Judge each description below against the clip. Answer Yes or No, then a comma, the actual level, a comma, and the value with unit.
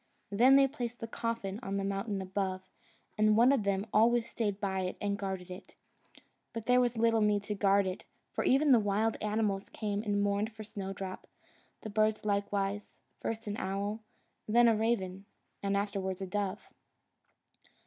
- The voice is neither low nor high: No, high, 205 Hz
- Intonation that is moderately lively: No, narrow, 2.3 semitones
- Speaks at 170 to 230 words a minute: Yes, average, 175 wpm